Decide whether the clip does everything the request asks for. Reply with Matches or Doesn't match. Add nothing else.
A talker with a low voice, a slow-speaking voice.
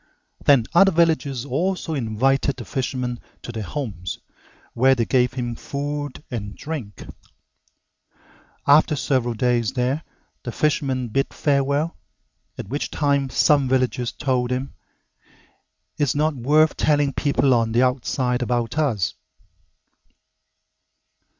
Matches